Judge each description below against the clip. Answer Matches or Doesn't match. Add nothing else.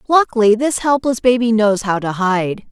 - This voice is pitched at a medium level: Doesn't match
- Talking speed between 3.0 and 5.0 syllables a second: Matches